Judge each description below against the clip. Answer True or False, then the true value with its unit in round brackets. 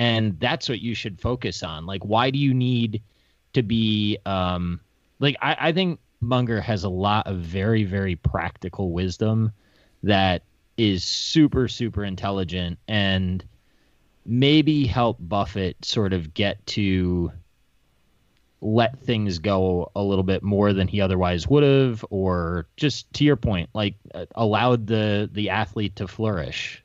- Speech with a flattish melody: False (3.8 semitones)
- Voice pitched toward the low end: True (105 Hz)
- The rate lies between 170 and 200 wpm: False (145 wpm)